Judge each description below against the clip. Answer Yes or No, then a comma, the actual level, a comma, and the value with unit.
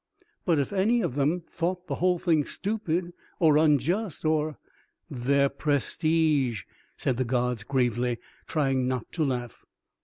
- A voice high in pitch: No, medium, 150 Hz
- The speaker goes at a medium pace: Yes, average, 145 wpm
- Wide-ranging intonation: No, average, 4.7 semitones